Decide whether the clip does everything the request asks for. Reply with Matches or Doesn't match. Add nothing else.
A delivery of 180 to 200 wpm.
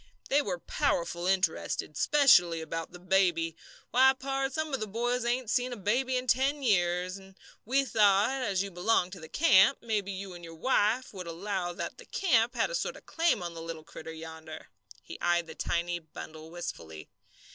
Matches